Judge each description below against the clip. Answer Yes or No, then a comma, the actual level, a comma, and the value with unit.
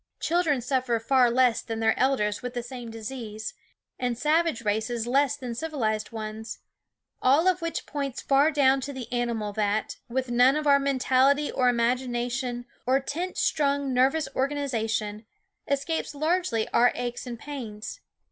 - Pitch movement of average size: Yes, average, 3.3 semitones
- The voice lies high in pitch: Yes, very high, 255 Hz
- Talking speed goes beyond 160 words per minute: No, average, 150 wpm